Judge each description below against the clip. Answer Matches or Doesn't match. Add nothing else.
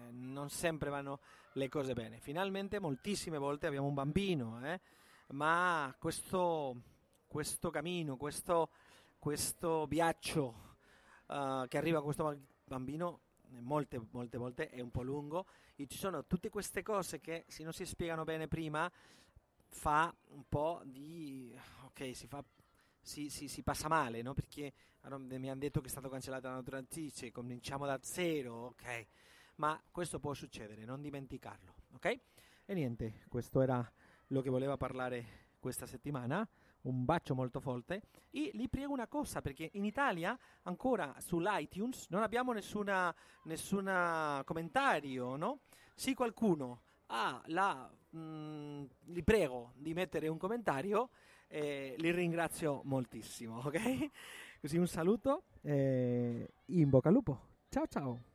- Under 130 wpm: Doesn't match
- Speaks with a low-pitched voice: Doesn't match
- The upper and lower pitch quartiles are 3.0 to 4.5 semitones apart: Doesn't match